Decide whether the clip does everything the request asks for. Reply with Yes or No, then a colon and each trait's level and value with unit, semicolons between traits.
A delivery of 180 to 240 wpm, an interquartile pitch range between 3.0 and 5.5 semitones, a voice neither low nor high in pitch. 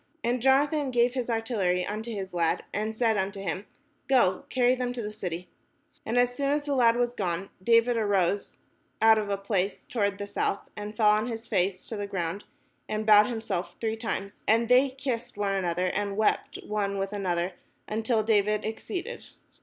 No: average, 185 wpm; average, 3.3 semitones; high, 215 Hz